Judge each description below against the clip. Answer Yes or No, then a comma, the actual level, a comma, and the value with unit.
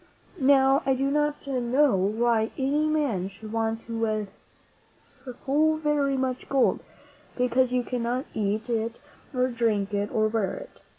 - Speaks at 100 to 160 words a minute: Yes, slow, 135 wpm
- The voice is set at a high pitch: Yes, very high, 250 Hz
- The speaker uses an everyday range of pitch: Yes, average, 3.7 semitones